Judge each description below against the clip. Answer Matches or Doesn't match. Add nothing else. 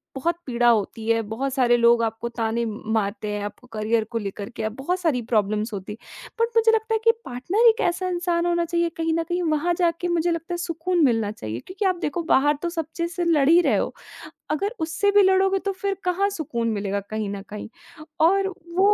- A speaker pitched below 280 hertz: Doesn't match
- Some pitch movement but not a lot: Doesn't match